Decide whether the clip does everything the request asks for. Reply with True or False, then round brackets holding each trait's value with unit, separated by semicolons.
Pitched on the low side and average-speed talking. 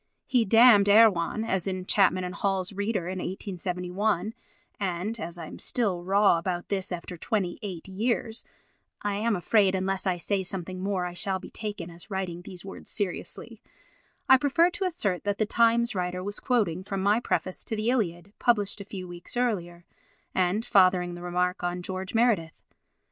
False (195 Hz; 170 wpm)